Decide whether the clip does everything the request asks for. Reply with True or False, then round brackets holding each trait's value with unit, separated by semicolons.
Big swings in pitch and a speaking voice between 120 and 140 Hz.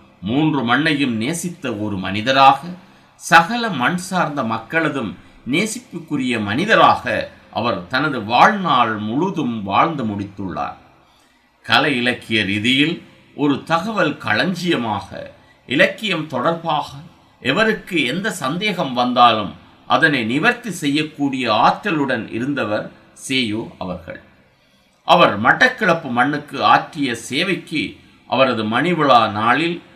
True (7.3 semitones; 135 Hz)